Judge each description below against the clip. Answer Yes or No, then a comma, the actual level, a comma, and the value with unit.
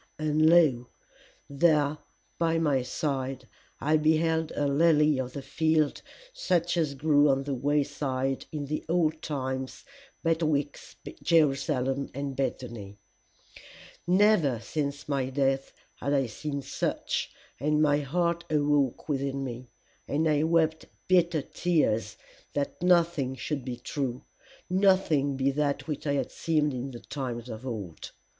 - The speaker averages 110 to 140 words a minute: Yes, slow, 135 wpm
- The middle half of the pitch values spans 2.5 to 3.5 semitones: Yes, average, 2.9 semitones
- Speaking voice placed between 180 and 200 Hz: No, medium, 145 Hz